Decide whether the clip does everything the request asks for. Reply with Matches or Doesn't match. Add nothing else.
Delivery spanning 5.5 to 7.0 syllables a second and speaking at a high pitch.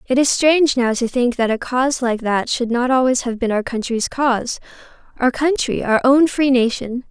Doesn't match